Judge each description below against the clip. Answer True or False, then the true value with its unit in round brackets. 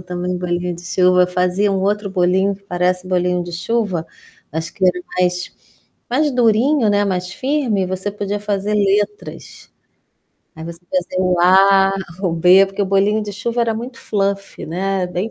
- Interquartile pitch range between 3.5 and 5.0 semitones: False (2.4 semitones)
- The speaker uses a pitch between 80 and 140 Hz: False (195 Hz)